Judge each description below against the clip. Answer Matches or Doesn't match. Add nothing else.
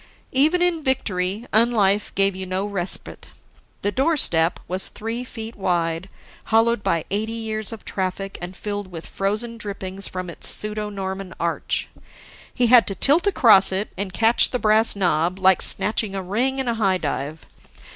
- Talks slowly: Doesn't match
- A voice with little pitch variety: Doesn't match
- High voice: Matches